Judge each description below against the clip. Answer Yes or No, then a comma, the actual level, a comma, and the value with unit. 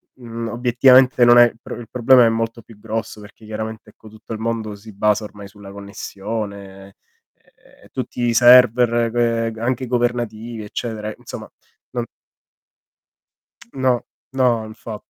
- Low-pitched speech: Yes, low, 115 Hz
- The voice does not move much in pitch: Yes, narrow, 2.1 semitones